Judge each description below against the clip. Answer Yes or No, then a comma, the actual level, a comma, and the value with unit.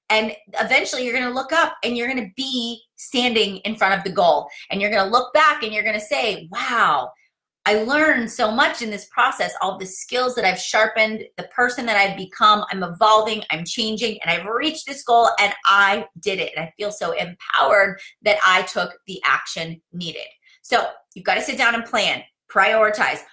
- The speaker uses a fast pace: No, average, 195 wpm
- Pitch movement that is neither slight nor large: Yes, average, 4.0 semitones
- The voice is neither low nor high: No, high, 220 Hz